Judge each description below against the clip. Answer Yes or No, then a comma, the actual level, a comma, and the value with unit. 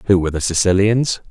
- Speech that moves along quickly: No, average, 185 wpm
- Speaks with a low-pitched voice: Yes, very low, 95 Hz